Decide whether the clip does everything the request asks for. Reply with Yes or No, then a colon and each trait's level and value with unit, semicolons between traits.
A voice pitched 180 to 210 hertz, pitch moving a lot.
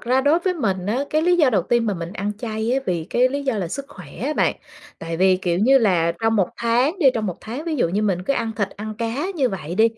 No: high, 225 Hz; wide, 6.0 semitones